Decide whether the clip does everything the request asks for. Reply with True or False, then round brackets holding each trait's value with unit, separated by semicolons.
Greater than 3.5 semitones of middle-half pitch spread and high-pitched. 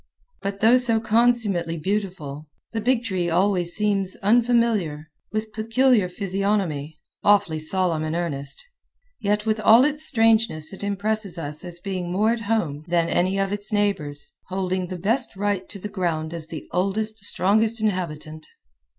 True (4.1 semitones; 195 Hz)